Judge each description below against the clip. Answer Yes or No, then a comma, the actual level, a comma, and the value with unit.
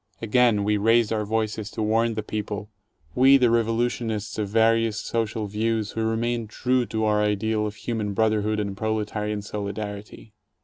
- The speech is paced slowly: No, average, 165 wpm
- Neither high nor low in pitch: No, low, 110 Hz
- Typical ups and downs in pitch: No, narrow, 1.4 semitones